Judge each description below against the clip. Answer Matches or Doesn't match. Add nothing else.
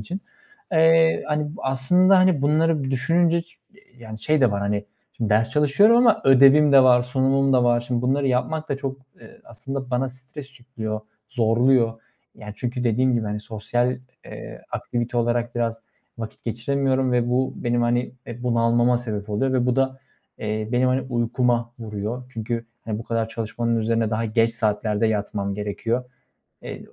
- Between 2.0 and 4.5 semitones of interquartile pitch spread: Matches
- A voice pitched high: Doesn't match